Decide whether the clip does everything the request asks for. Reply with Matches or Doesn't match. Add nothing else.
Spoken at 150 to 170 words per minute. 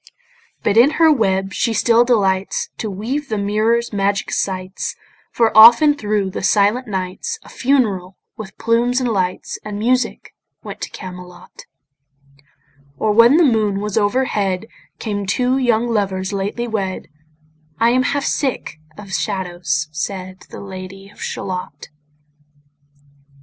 Doesn't match